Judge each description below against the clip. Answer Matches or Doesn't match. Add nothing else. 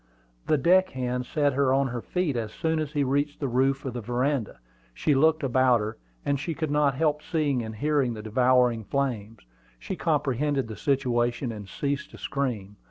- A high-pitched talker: Doesn't match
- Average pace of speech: Matches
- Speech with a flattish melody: Doesn't match